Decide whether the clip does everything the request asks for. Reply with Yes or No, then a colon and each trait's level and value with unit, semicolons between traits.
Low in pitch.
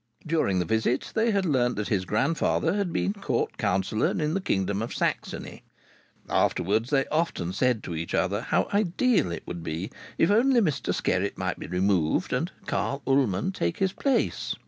Yes: low, 125 Hz